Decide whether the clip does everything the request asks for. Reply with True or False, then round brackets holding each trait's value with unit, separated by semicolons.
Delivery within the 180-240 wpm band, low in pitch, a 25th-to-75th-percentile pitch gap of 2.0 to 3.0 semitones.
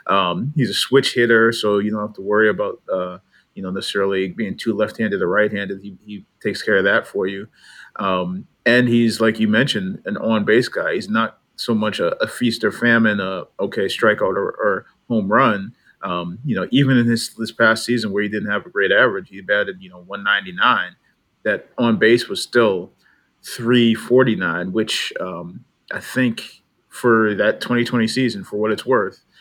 True (200 wpm; 110 Hz; 2.7 semitones)